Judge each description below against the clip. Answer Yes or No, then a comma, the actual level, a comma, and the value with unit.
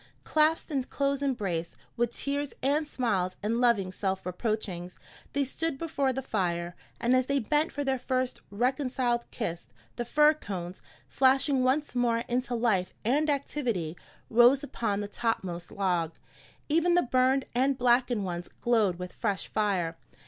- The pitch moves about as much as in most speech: No, wide, 5.8 semitones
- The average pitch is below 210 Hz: No, high, 240 Hz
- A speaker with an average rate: Yes, average, 150 wpm